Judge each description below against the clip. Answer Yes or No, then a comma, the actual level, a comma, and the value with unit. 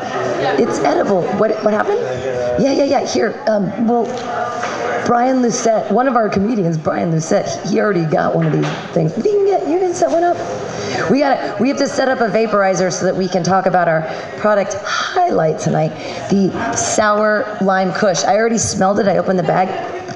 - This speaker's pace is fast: No, average, 195 wpm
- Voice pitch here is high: Yes, high, 215 Hz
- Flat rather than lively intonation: No, average, 4.3 semitones